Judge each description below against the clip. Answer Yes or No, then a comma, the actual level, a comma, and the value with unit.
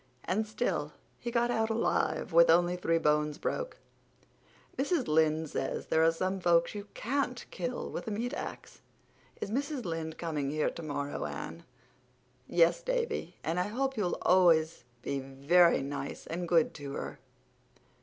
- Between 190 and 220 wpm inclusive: No, average, 155 wpm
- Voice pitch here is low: No, medium, 170 Hz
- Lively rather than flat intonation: Yes, wide, 5.9 semitones